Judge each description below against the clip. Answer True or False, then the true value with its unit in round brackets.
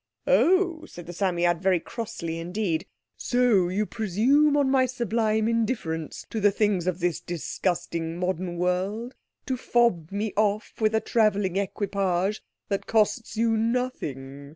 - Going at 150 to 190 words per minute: False (140 wpm)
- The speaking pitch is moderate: False (205 Hz)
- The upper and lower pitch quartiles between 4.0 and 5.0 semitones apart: True (4.6 semitones)